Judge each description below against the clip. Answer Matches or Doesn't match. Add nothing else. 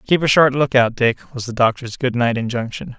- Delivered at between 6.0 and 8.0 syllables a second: Doesn't match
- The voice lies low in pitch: Matches